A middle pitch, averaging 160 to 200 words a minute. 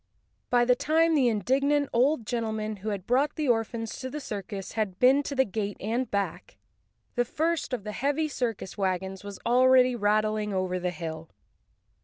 No: high, 230 Hz; average, 175 wpm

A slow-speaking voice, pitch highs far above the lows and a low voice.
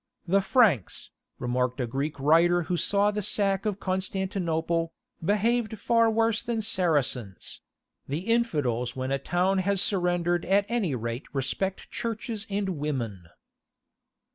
No: slow, 130 wpm; wide, 6.4 semitones; medium, 180 Hz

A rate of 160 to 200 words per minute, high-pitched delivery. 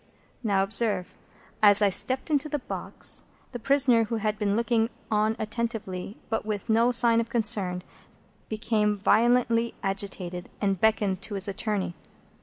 No: average, 145 wpm; high, 215 Hz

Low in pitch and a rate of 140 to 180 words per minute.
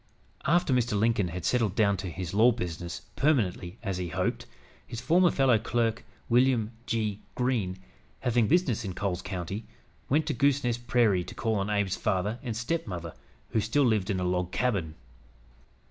Yes: low, 110 Hz; average, 165 wpm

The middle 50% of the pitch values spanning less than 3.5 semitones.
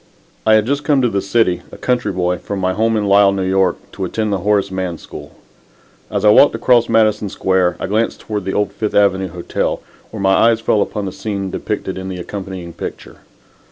Yes: narrow, 2.5 semitones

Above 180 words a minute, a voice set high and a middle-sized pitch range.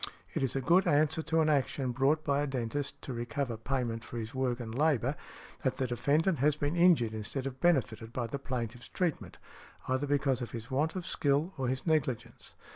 No: average, 200 wpm; low, 135 Hz; average, 3.7 semitones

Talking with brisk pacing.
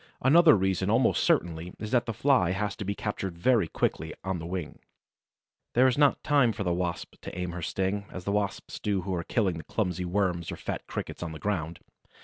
Yes: fast, 210 wpm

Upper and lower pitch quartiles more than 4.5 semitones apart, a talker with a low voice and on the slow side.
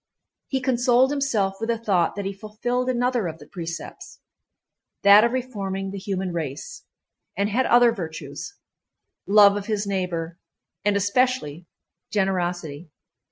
No: average, 4.9 semitones; high, 200 Hz; slow, 120 wpm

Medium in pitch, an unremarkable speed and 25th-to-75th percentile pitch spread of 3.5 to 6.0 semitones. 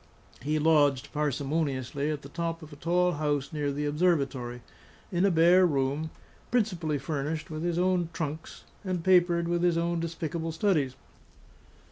No: medium, 160 Hz; average, 150 wpm; average, 3.0 semitones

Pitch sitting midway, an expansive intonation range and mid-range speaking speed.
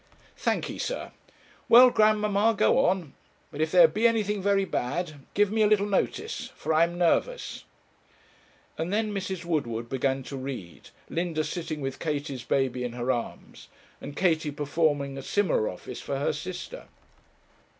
Yes: medium, 170 Hz; wide, 6.8 semitones; average, 155 wpm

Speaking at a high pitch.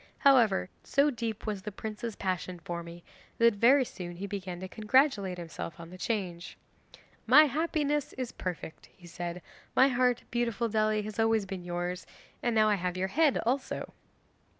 Yes: high, 210 Hz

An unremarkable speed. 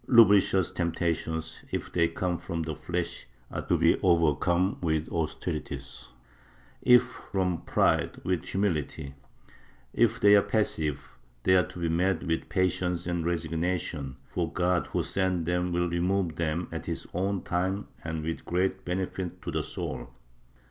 Yes: average, 150 wpm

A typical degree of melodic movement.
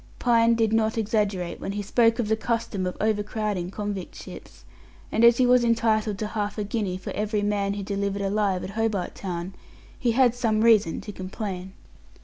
No: narrow, 2.3 semitones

